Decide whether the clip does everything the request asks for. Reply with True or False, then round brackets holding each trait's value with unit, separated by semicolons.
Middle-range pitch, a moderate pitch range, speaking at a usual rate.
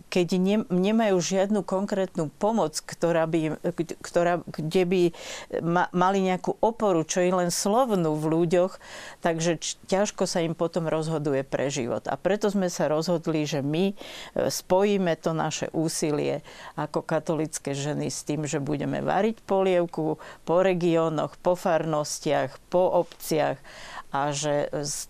True (175 Hz; 3.1 semitones; 135 wpm)